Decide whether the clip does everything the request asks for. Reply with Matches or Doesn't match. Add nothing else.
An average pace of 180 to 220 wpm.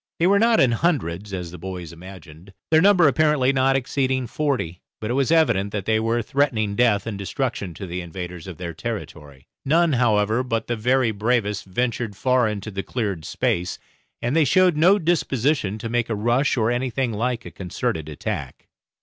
Matches